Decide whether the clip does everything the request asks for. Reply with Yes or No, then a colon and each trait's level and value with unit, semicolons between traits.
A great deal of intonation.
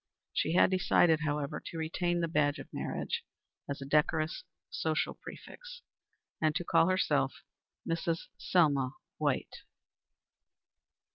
No: average, 2.8 semitones